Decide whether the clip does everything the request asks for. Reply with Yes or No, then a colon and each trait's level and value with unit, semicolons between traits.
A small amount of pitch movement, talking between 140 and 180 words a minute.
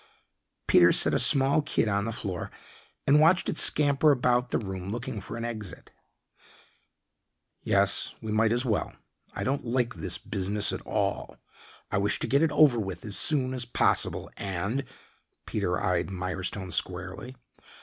No: wide, 5.4 semitones; average, 160 wpm